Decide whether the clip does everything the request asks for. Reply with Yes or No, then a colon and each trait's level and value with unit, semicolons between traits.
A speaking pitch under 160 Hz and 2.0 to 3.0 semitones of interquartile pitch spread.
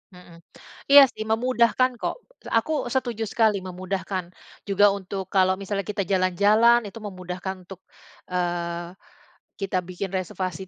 No: high, 190 Hz; narrow, 2.5 semitones